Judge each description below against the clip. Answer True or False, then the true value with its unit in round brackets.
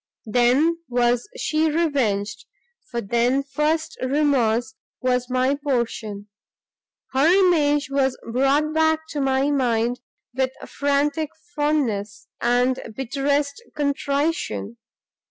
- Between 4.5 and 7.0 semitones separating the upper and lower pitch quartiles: False (3.4 semitones)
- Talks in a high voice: True (275 Hz)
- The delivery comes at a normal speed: False (100 wpm)